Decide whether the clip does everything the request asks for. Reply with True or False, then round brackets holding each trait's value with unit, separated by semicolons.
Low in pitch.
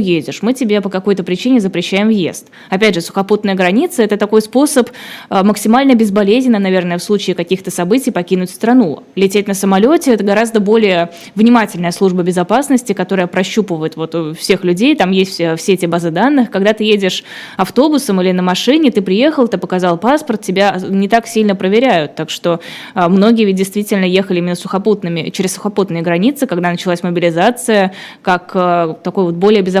False (195 Hz)